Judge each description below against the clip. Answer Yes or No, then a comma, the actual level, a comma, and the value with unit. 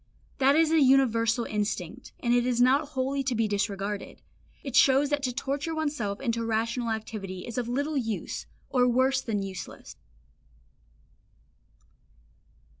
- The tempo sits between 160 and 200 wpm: No, average, 140 wpm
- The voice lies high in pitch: Yes, high, 245 Hz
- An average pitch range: Yes, average, 3.7 semitones